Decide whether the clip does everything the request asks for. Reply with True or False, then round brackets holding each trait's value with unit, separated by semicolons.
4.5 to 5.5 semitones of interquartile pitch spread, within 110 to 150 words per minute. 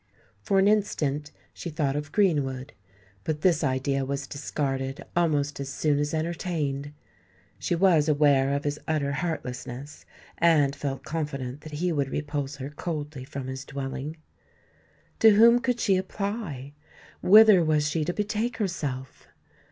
False (3.8 semitones; 145 wpm)